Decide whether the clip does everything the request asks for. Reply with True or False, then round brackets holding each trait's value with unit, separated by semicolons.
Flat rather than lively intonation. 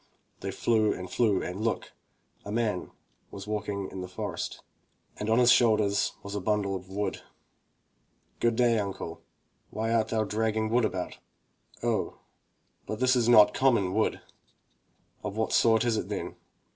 True (2.3 semitones)